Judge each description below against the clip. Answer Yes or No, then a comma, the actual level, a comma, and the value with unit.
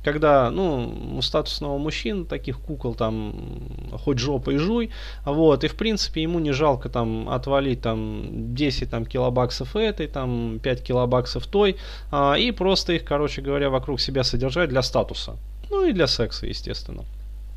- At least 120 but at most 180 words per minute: Yes, average, 155 wpm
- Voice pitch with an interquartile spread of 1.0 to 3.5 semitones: No, average, 4.0 semitones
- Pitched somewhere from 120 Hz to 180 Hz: Yes, low, 135 Hz